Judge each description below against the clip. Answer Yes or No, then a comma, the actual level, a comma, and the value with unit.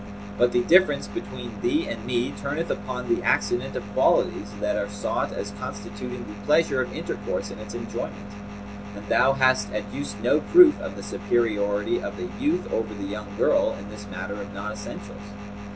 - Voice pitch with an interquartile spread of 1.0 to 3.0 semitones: No, average, 3.7 semitones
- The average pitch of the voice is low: Yes, low, 105 Hz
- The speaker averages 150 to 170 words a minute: No, average, 180 wpm